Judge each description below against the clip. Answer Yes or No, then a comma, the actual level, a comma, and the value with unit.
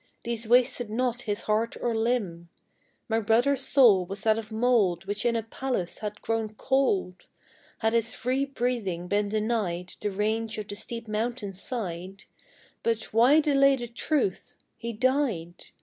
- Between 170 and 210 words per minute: No, average, 155 wpm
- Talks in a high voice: Yes, high, 225 Hz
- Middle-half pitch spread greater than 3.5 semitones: No, average, 3.1 semitones